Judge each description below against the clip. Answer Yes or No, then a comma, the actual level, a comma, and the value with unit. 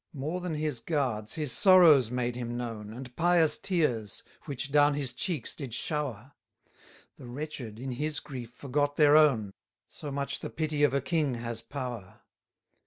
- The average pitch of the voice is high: No, medium, 140 Hz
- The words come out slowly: No, average, 170 wpm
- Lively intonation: No, average, 3.9 semitones